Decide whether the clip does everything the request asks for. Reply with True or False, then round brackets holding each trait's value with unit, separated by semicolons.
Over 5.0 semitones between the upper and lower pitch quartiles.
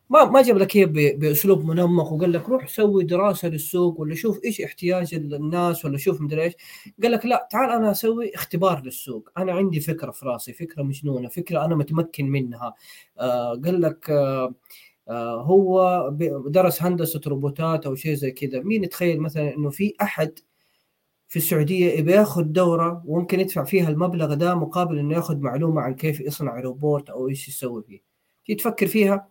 False (4.5 semitones)